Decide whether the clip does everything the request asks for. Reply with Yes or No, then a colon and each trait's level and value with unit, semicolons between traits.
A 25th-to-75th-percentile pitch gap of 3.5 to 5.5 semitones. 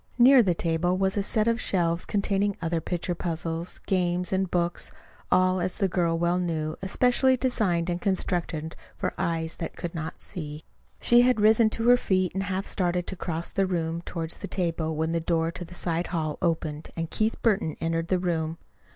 No: average, 2.7 semitones